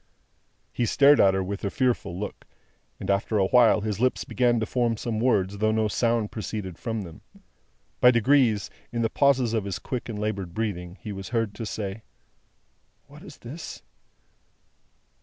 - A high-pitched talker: No, low, 110 Hz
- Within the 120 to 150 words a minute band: No, average, 175 wpm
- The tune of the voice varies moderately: Yes, average, 3.1 semitones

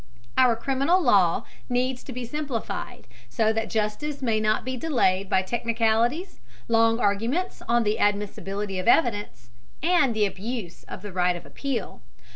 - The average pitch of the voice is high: Yes, high, 225 Hz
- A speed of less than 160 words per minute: Yes, average, 150 wpm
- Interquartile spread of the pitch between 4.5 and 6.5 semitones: No, average, 3.8 semitones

